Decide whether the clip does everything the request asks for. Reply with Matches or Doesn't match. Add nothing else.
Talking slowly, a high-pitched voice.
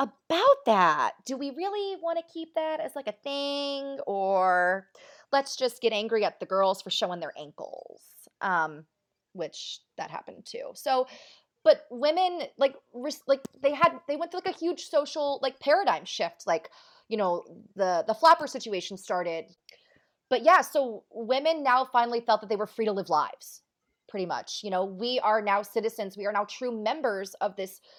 Doesn't match